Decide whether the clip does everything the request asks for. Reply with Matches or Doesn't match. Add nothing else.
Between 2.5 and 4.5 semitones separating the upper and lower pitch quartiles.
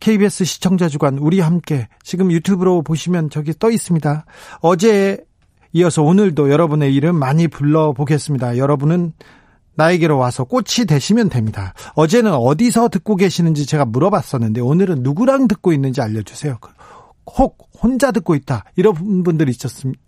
Doesn't match